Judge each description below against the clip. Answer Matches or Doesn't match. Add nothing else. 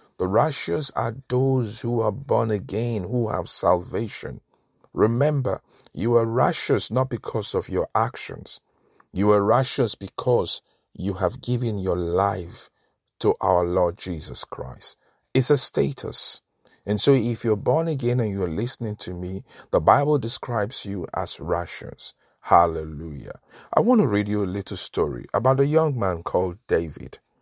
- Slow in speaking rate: Doesn't match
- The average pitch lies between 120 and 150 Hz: Doesn't match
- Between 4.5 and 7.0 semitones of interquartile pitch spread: Matches